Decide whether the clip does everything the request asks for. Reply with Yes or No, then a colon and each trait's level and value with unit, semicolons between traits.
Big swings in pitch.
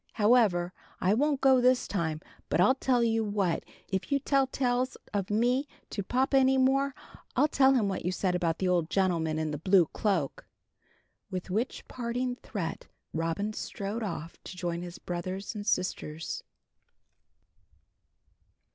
Yes: wide, 6.2 semitones